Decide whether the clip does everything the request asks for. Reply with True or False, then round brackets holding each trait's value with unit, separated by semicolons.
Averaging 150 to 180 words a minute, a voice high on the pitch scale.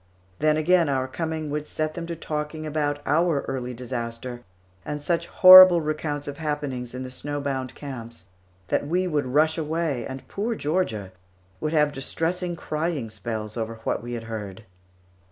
False (165 wpm; 145 Hz)